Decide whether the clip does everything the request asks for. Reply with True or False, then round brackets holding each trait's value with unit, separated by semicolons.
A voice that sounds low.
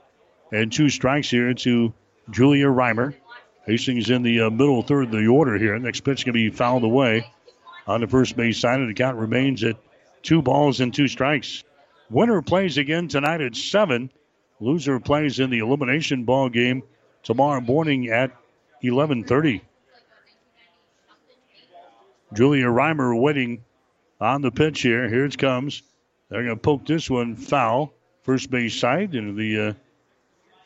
True (130 Hz)